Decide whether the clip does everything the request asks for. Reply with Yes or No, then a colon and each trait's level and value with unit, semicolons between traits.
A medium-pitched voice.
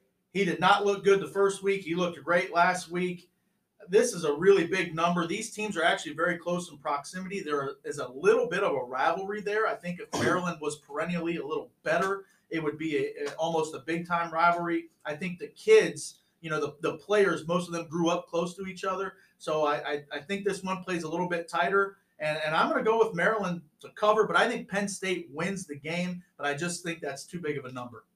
Yes: medium, 175 Hz